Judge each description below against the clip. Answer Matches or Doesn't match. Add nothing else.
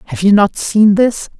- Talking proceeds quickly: Matches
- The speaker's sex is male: Doesn't match